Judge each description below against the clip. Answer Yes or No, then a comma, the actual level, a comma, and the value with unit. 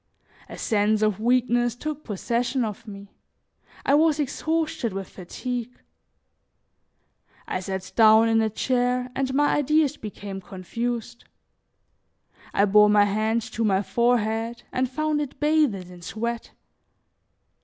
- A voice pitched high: Yes, high, 230 Hz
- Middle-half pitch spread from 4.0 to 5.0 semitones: No, average, 3.5 semitones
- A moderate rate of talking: No, slow, 125 wpm